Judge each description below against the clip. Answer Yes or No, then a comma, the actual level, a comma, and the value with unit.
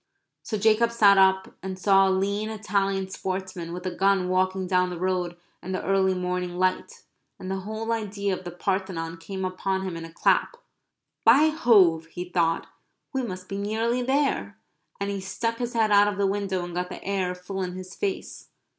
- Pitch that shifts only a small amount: Yes, narrow, 2.1 semitones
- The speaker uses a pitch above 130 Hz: Yes, high, 190 Hz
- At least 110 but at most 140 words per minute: No, average, 195 wpm